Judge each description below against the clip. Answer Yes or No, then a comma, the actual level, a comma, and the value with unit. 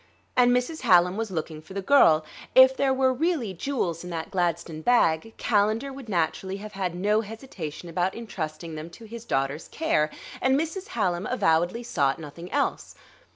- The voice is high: Yes, high, 195 Hz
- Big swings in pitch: Yes, wide, 6.8 semitones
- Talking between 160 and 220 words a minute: Yes, average, 170 wpm